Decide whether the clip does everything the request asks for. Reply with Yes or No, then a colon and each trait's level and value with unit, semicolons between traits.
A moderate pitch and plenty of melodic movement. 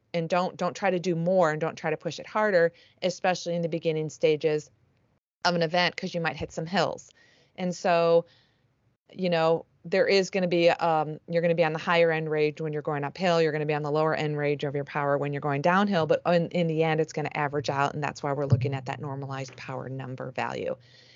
No: medium, 160 Hz; average, 3.1 semitones